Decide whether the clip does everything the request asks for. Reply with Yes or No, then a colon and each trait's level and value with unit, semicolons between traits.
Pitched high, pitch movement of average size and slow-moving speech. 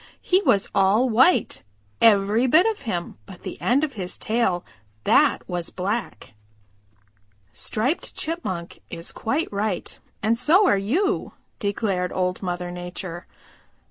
No: high, 205 Hz; wide, 6.0 semitones; slow, 130 wpm